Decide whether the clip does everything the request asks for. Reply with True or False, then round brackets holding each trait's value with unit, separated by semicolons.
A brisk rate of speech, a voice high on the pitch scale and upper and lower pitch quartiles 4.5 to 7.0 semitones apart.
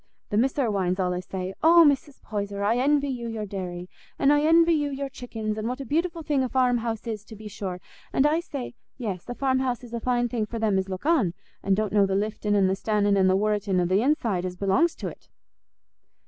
True (235 wpm; 225 Hz; 5.3 semitones)